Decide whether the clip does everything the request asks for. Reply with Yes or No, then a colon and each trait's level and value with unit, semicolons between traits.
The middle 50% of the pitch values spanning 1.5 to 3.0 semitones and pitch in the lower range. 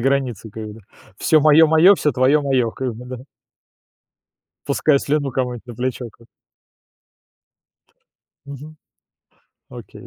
No: average, 3.5 semitones; low, 130 Hz